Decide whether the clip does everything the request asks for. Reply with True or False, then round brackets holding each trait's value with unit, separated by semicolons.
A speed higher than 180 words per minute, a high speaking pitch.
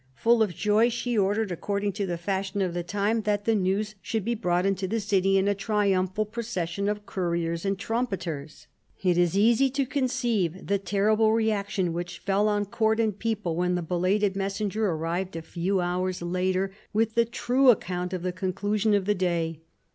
True (190 wpm; 195 Hz)